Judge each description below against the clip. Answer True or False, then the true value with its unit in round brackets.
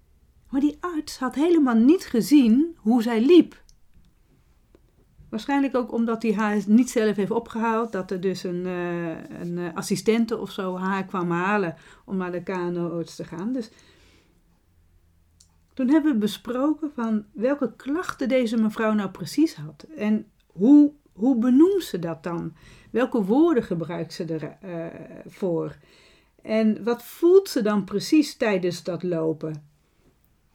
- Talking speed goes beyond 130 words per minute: True (140 wpm)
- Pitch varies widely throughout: True (6.5 semitones)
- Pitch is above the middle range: True (210 Hz)